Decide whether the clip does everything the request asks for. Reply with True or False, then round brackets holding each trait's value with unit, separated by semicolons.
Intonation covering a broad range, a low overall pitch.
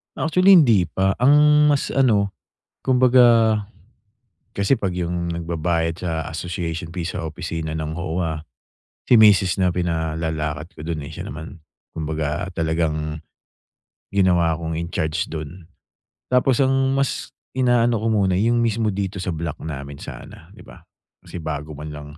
True (5.9 semitones; 85 Hz)